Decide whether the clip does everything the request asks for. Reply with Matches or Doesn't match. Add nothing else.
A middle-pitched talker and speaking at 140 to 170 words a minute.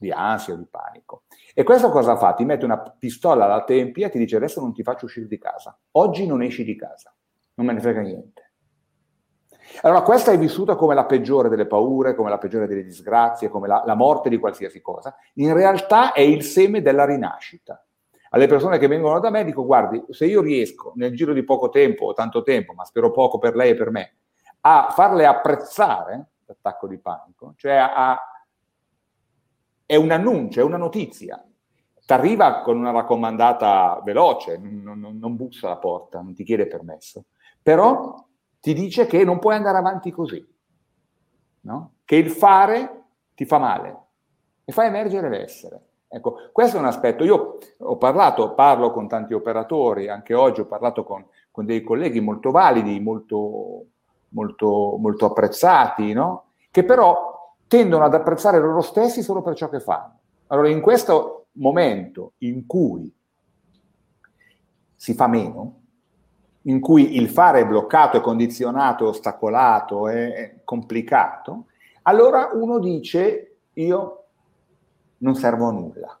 Matches